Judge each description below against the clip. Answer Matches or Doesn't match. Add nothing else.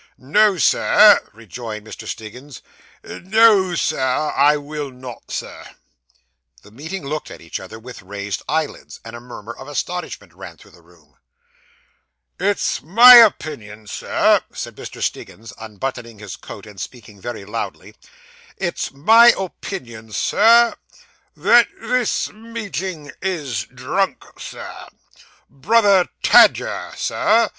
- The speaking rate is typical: Doesn't match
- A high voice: Doesn't match